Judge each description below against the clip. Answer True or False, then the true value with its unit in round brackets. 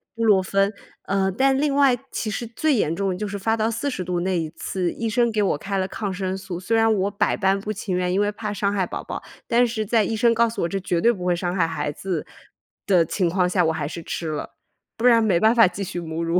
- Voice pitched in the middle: False (195 Hz)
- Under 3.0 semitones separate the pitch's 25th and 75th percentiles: False (3.9 semitones)